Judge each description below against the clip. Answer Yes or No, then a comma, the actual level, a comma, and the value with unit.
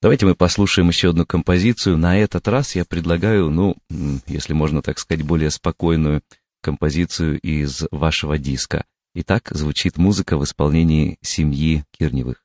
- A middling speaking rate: Yes, average, 140 wpm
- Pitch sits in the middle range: No, very low, 80 Hz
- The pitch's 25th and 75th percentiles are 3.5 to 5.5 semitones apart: No, average, 3.1 semitones